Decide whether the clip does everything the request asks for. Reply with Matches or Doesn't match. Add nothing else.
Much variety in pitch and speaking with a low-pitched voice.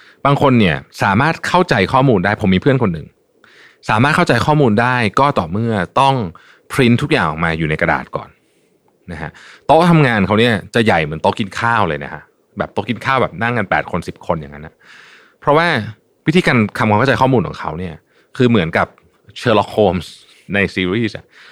Matches